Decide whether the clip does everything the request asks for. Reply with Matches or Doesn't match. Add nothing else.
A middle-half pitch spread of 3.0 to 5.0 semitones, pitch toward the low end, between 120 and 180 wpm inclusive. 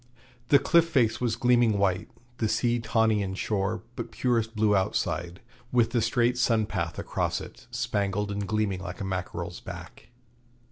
Matches